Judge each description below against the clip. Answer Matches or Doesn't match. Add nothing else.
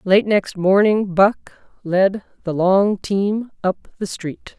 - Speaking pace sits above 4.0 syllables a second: Doesn't match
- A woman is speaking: Matches